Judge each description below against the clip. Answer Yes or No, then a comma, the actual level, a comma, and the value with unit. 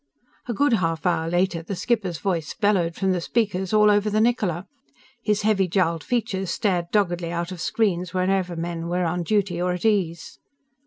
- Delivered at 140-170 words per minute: No, average, 180 wpm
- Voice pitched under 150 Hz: No, medium, 185 Hz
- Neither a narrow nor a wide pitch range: Yes, average, 3.3 semitones